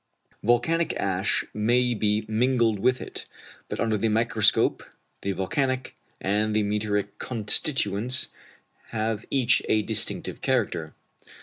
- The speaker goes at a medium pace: No, slow, 115 wpm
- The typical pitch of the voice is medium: No, low, 110 Hz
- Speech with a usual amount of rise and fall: Yes, average, 3.0 semitones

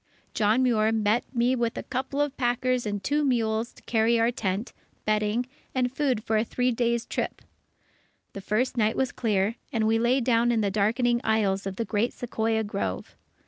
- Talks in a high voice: Yes, high, 230 Hz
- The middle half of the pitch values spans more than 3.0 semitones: No, narrow, 2.5 semitones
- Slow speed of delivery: No, average, 185 wpm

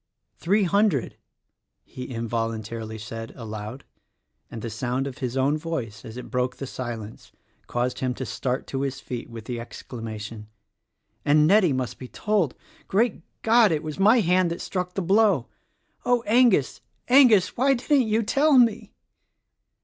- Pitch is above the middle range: No, medium, 140 Hz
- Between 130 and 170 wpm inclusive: Yes, average, 155 wpm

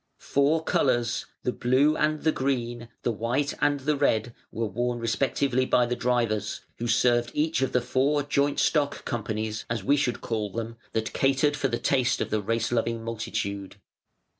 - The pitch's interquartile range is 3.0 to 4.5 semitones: Yes, average, 3.4 semitones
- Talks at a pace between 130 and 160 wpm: No, average, 175 wpm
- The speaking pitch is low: Yes, low, 120 Hz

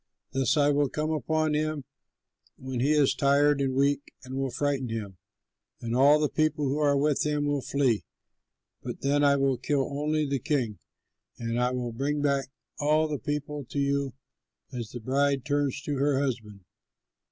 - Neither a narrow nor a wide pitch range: No, narrow, 2.0 semitones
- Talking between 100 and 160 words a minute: No, average, 175 wpm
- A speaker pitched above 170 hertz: No, medium, 140 Hz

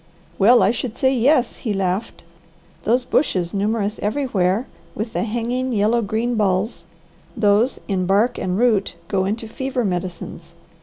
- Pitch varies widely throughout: No, average, 3.6 semitones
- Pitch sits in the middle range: No, high, 220 Hz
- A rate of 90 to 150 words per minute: Yes, average, 145 wpm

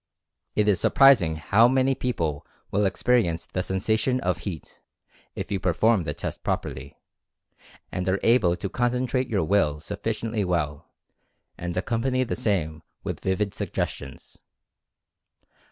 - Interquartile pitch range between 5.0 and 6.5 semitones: Yes, average, 5.3 semitones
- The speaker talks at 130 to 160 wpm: Yes, slow, 135 wpm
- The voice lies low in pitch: Yes, low, 100 Hz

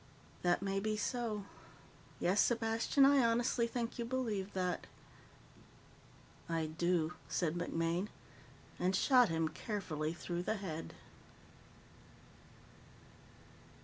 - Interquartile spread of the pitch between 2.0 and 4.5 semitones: No, average, 5.2 semitones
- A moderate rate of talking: No, slow, 100 wpm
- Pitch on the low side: No, high, 195 Hz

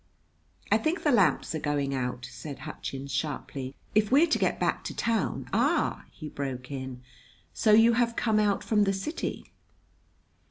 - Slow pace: No, average, 170 wpm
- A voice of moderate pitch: Yes, medium, 160 Hz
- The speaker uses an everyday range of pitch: No, wide, 8.8 semitones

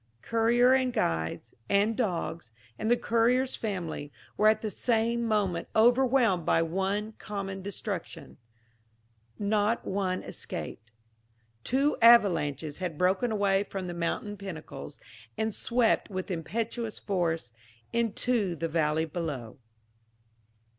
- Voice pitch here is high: Yes, high, 200 Hz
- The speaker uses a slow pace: Yes, slow, 115 wpm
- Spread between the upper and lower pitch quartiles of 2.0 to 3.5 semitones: No, average, 5.2 semitones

